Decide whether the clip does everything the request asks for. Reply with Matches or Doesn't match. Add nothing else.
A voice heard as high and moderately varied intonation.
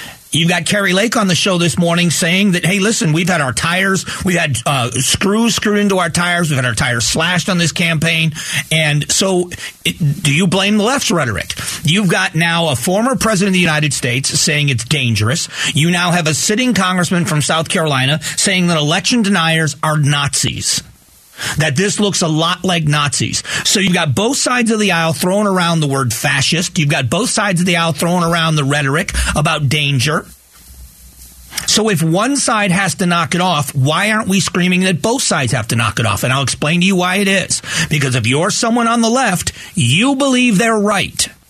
Doesn't match